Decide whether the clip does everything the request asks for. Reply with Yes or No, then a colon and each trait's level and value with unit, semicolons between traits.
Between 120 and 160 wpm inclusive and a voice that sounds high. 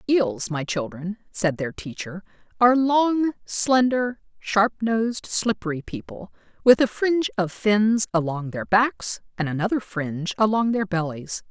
Yes: average, 140 wpm; high, 200 Hz